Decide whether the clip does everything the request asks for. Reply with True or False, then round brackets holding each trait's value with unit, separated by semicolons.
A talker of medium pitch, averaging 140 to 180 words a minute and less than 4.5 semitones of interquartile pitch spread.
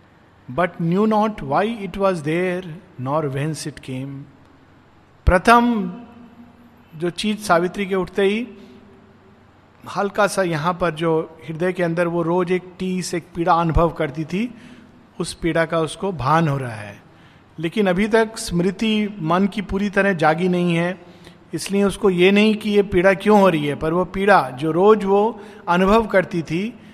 True (180 Hz; 165 wpm; 3.8 semitones)